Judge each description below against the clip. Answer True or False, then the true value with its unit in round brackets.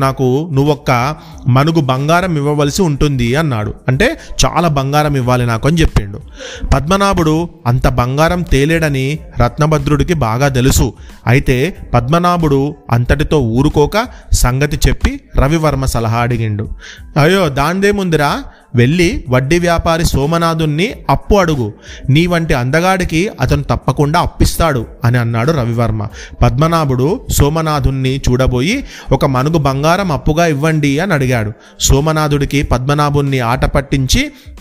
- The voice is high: False (145 Hz)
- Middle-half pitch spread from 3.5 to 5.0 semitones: True (4.0 semitones)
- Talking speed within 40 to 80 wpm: False (105 wpm)